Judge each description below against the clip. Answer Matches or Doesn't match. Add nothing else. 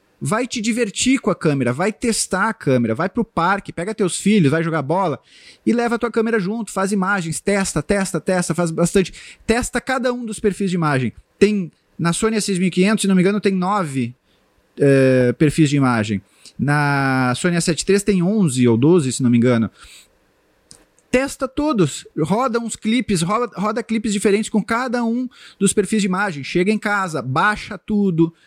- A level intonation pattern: Doesn't match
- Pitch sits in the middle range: Doesn't match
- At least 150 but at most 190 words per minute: Matches